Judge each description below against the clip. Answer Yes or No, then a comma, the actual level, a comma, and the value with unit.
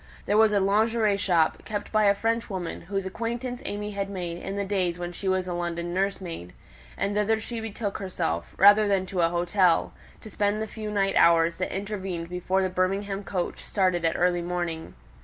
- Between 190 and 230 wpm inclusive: Yes, average, 195 wpm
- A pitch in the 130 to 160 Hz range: No, high, 195 Hz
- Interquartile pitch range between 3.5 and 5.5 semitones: No, average, 2.8 semitones